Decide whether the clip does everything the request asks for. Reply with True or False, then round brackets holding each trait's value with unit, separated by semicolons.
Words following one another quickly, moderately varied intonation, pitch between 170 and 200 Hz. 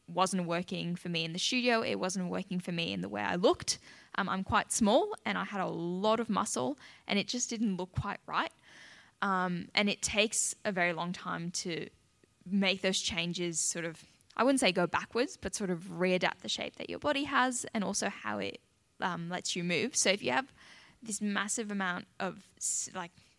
True (210 wpm; 3.5 semitones; 185 Hz)